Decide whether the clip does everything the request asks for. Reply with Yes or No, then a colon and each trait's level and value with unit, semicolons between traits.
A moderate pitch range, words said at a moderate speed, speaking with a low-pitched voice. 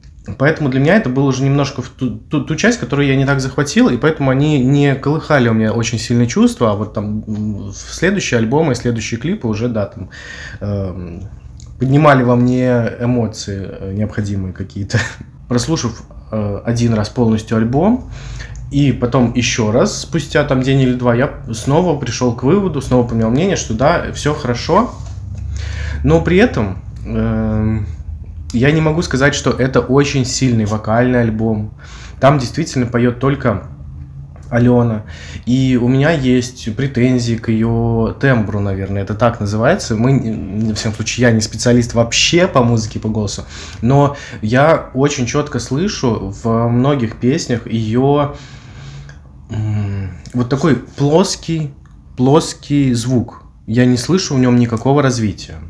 Yes: average, 4.0 semitones; average, 150 wpm; low, 120 Hz